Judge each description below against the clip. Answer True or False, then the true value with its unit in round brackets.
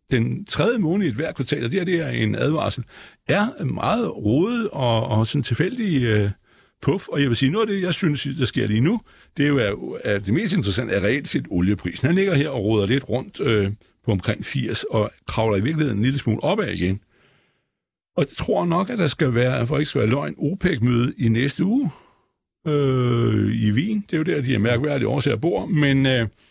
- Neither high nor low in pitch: False (130 Hz)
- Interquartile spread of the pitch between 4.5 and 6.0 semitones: True (5.5 semitones)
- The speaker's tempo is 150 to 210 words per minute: False (225 wpm)